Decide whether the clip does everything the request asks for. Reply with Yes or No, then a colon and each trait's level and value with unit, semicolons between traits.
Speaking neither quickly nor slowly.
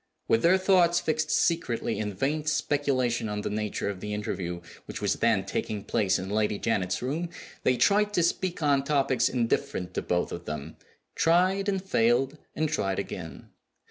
Yes: average, 175 wpm